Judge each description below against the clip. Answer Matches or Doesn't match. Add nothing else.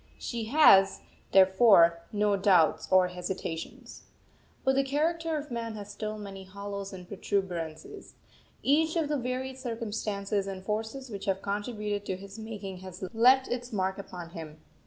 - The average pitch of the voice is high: Matches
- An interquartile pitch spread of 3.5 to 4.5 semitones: Matches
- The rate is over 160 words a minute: Doesn't match